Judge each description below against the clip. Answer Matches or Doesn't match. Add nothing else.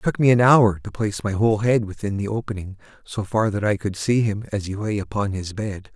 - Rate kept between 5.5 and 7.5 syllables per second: Matches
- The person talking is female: Doesn't match